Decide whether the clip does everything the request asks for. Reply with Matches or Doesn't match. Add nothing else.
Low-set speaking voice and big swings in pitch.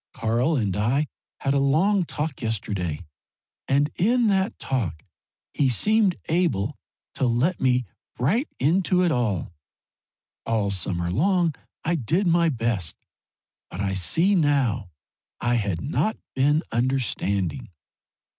Matches